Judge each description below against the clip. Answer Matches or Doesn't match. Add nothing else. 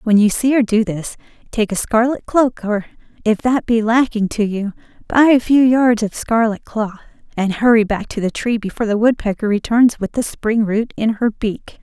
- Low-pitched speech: Doesn't match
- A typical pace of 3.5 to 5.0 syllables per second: Matches